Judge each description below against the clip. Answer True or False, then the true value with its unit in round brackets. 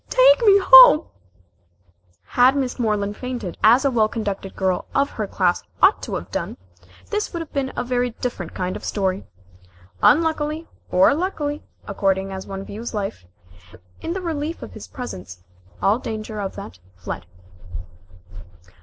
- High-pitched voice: True (225 Hz)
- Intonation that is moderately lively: False (7.3 semitones)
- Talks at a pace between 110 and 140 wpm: False (160 wpm)